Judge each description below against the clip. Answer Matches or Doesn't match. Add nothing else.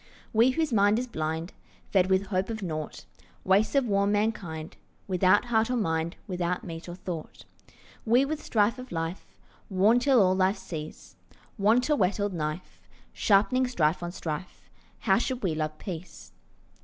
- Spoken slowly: Doesn't match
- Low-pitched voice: Doesn't match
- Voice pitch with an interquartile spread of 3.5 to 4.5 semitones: Doesn't match